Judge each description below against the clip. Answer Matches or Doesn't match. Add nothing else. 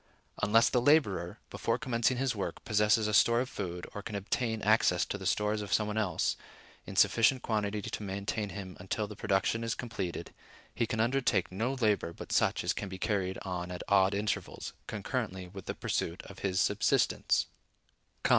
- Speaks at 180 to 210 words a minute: Matches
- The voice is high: Doesn't match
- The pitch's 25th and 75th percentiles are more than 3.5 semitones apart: Doesn't match